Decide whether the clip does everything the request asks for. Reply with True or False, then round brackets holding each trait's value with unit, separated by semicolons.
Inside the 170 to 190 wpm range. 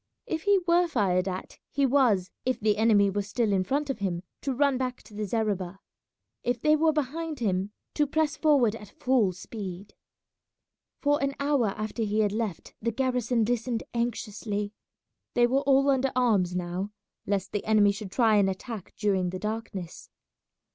True (175 wpm)